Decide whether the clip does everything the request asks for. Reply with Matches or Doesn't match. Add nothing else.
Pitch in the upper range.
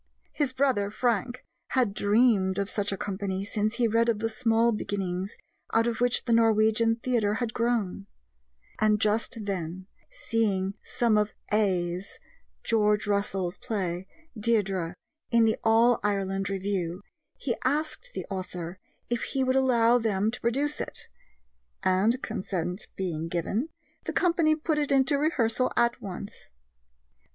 Matches